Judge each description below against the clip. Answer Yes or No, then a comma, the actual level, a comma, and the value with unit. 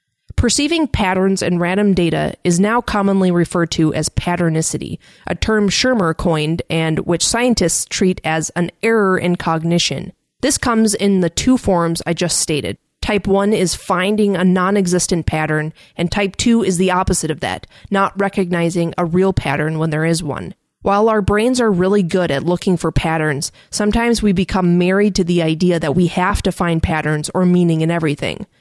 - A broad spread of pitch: No, average, 3.4 semitones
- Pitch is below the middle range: No, medium, 180 Hz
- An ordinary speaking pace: Yes, average, 180 wpm